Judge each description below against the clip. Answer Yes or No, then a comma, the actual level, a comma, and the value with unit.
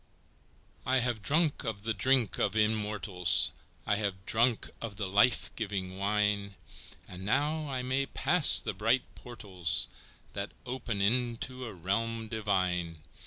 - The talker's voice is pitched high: No, low, 110 Hz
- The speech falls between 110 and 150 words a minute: Yes, average, 140 wpm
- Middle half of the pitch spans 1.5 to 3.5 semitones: No, average, 4.0 semitones